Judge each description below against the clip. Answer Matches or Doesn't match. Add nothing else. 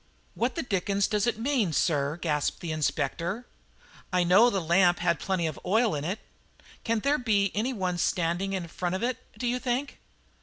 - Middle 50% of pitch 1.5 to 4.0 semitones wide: Doesn't match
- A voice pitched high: Matches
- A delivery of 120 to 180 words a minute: Doesn't match